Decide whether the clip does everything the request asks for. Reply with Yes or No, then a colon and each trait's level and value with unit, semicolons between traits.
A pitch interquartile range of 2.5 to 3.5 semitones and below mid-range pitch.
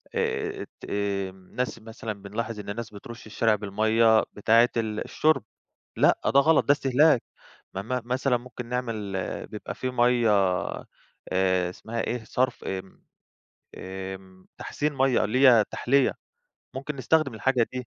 No: average, 4.0 semitones; low, 115 Hz